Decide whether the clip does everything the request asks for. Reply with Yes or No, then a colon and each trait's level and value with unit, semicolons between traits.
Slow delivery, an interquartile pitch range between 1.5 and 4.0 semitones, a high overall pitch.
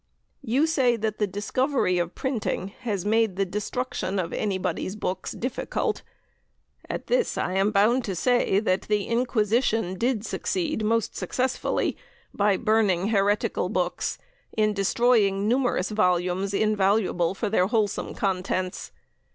Yes: slow, 130 wpm; average, 3.5 semitones; high, 210 Hz